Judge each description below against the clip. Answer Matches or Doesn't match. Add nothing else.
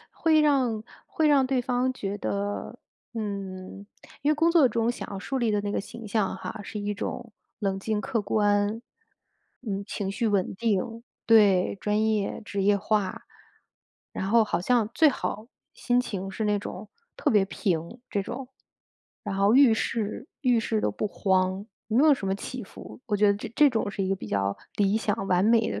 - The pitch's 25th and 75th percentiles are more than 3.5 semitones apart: Doesn't match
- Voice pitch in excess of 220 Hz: Doesn't match